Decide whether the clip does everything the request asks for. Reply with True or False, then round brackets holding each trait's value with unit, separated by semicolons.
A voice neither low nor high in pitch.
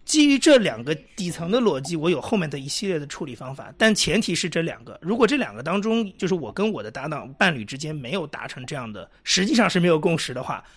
True (175 Hz)